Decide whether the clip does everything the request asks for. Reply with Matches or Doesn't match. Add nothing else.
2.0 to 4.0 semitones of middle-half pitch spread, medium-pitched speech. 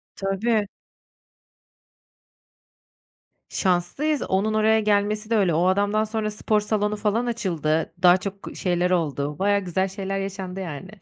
Doesn't match